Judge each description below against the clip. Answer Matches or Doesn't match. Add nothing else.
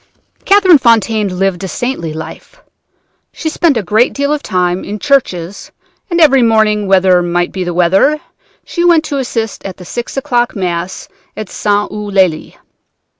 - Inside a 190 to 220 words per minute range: Doesn't match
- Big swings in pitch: Matches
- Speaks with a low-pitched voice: Doesn't match